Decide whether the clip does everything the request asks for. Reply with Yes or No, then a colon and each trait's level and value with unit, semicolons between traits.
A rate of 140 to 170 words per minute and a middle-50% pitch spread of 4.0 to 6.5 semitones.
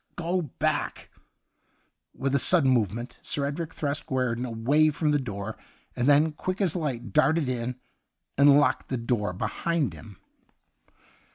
Yes: average, 160 wpm; average, 4.3 semitones